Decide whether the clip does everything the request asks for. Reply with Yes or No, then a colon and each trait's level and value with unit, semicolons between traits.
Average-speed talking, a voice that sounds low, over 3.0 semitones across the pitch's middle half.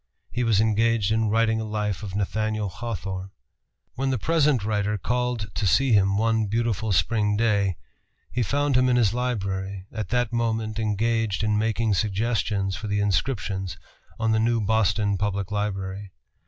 No: average, 160 wpm; low, 110 Hz; narrow, 2.4 semitones